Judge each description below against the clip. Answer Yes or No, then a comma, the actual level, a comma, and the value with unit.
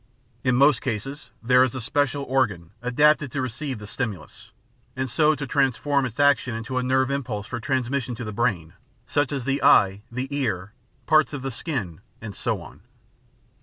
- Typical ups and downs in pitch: Yes, average, 3.7 semitones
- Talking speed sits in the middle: Yes, average, 180 wpm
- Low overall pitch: Yes, low, 130 Hz